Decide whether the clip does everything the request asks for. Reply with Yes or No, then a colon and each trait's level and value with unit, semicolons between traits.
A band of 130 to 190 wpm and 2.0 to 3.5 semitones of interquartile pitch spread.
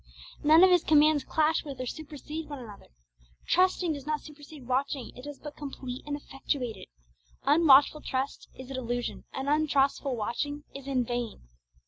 Yes: average, 165 wpm; average, 2.8 semitones